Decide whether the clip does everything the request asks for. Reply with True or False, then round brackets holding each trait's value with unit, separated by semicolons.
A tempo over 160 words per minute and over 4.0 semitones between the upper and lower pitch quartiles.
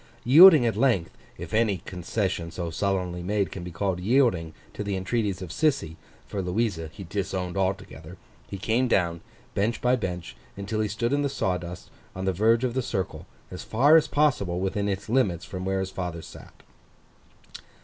True (170 wpm; 4.4 semitones)